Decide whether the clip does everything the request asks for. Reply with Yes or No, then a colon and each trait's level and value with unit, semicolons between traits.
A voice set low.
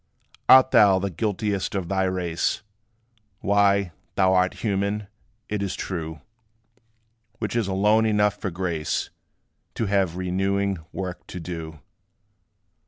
Yes: very low, 95 Hz